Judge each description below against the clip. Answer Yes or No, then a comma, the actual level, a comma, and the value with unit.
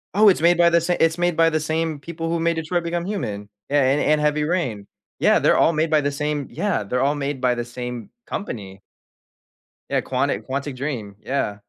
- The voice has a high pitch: No, medium, 150 Hz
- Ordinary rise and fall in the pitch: Yes, average, 4.7 semitones